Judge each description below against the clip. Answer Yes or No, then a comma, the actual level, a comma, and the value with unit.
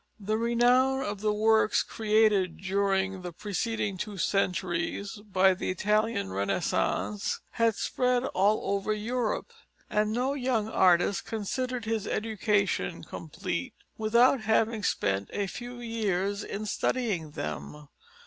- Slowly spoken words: Yes, slow, 120 wpm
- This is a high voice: Yes, high, 210 Hz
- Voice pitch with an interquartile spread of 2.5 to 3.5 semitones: Yes, average, 2.9 semitones